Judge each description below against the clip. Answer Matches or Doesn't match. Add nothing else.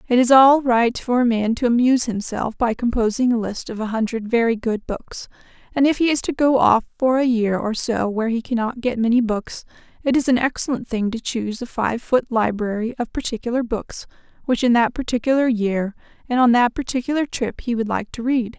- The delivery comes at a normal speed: Doesn't match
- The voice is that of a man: Doesn't match